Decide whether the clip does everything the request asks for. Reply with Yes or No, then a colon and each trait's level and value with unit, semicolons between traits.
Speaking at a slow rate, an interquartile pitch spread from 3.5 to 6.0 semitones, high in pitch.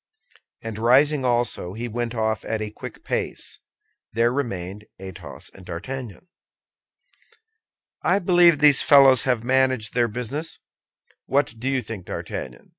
No: slow, 130 wpm; average, 3.9 semitones; low, 120 Hz